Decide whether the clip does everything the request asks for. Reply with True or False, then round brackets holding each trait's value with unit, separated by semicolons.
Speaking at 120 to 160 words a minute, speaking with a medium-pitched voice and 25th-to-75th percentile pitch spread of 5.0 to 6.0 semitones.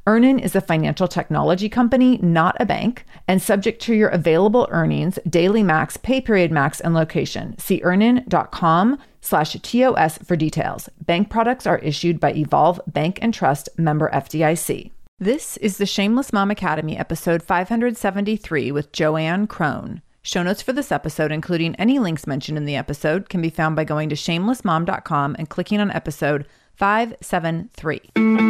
True (155 wpm; 180 Hz; 5.4 semitones)